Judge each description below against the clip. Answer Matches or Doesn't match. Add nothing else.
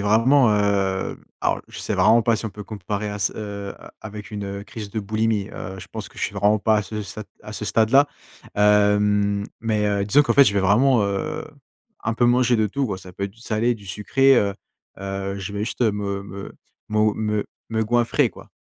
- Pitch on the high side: Doesn't match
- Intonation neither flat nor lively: Doesn't match